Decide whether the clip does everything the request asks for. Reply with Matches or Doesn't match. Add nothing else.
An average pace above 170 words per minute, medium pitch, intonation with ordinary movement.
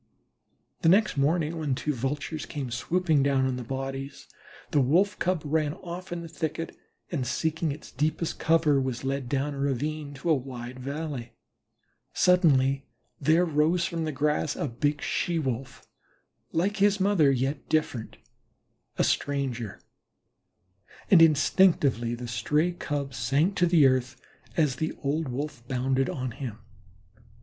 Doesn't match